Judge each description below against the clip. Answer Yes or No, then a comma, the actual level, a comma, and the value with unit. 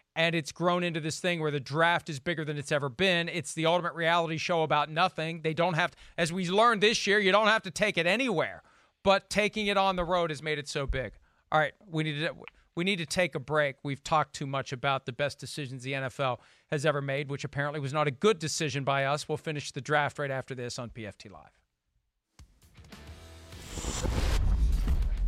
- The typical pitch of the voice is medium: Yes, medium, 155 Hz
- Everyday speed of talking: No, fast, 220 wpm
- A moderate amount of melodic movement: Yes, average, 4.0 semitones